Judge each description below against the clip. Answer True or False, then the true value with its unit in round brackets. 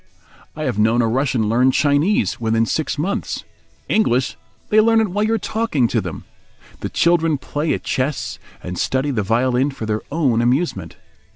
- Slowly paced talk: False (175 wpm)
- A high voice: False (130 Hz)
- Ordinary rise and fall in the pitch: False (6.1 semitones)